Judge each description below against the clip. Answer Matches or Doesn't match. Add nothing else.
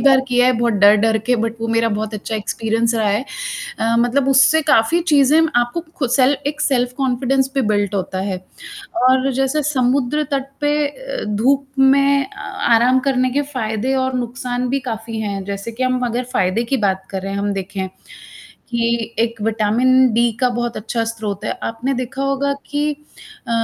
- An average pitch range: Matches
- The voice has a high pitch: Matches